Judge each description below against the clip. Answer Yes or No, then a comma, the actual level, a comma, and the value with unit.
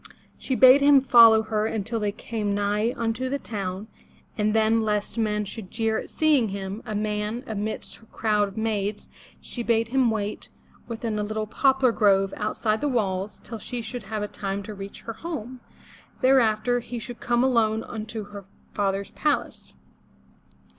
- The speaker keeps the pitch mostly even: Yes, narrow, 2.3 semitones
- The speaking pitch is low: No, high, 220 Hz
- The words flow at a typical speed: Yes, average, 170 wpm